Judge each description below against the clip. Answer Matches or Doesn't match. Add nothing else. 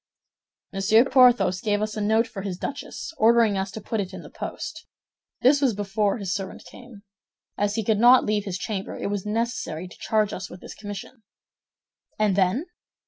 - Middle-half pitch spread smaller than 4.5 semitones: Matches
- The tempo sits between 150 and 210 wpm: Matches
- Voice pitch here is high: Matches